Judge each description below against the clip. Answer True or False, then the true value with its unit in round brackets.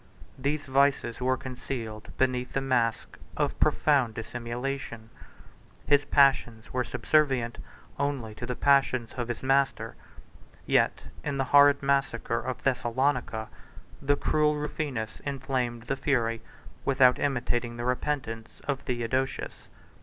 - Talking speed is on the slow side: True (125 wpm)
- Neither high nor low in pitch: False (130 Hz)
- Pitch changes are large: False (2.7 semitones)